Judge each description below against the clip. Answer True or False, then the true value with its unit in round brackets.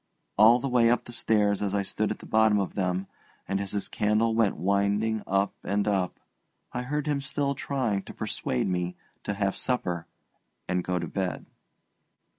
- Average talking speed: True (190 wpm)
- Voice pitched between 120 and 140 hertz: False (105 Hz)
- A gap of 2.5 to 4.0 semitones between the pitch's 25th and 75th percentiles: True (3.0 semitones)